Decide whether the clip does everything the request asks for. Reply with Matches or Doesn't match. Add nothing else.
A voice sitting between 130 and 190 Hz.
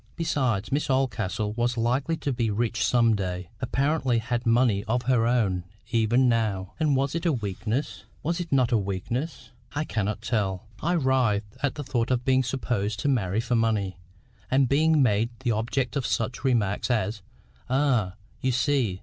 Doesn't match